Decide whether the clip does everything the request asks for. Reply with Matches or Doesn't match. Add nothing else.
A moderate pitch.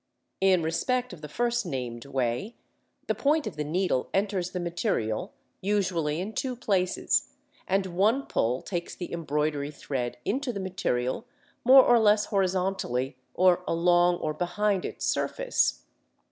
Matches